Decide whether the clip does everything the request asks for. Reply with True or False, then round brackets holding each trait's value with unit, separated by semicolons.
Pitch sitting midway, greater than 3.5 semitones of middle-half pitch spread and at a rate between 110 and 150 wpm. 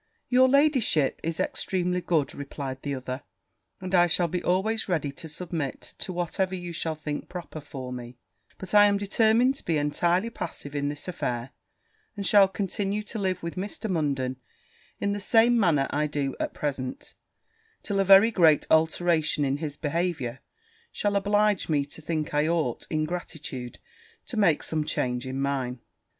False (165 Hz; 5.2 semitones; 170 wpm)